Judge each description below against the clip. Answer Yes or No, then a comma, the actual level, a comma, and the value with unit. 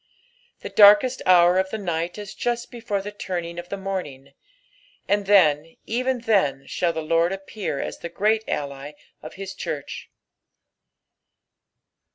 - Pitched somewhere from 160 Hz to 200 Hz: Yes, high, 190 Hz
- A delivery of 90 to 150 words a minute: Yes, average, 145 wpm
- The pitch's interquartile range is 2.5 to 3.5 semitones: No, average, 4.0 semitones